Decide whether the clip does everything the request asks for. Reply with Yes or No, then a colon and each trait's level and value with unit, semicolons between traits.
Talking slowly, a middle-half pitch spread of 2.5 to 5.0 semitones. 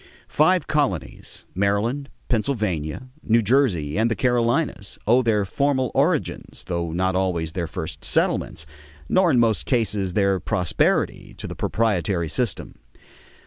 No: slow, 130 wpm; wide, 5.6 semitones